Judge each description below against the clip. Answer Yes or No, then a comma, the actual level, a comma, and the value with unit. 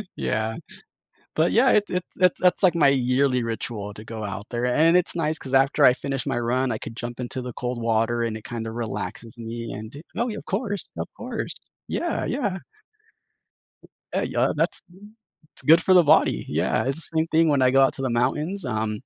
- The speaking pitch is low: Yes, low, 130 Hz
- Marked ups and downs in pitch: Yes, wide, 5.8 semitones